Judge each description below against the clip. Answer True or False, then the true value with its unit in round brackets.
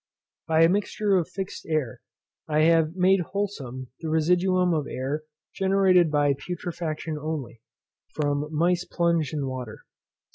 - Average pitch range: True (3.3 semitones)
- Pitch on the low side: False (160 Hz)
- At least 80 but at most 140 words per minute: True (135 wpm)